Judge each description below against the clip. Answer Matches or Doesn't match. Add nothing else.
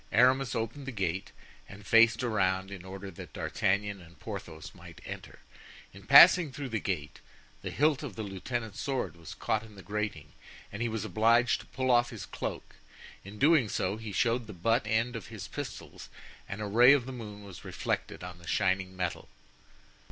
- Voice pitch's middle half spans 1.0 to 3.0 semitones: Doesn't match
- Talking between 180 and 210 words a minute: Matches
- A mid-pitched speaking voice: Doesn't match